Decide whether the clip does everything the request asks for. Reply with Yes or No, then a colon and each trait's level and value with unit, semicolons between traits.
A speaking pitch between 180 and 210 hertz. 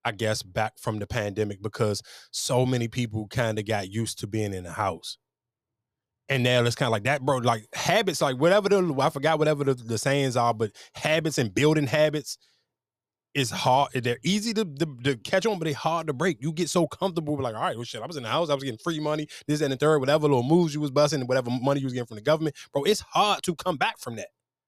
No: low, 135 Hz